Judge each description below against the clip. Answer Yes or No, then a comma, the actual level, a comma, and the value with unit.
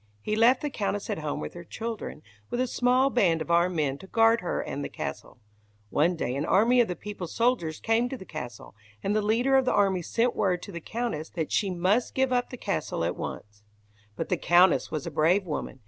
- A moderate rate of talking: No, fast, 230 wpm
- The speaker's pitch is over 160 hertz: Yes, high, 190 Hz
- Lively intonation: Yes, wide, 6.3 semitones